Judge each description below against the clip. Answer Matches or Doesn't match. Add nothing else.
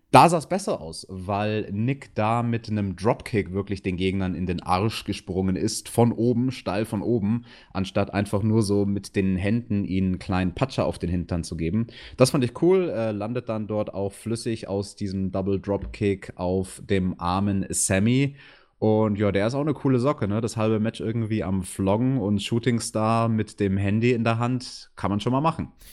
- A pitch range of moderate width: Matches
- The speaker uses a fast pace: Matches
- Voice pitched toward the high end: Doesn't match